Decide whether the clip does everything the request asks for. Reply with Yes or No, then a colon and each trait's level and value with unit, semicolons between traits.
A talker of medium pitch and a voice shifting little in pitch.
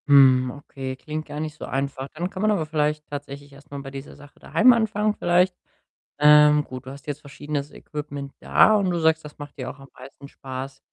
Yes: medium, 145 Hz; narrow, 2.2 semitones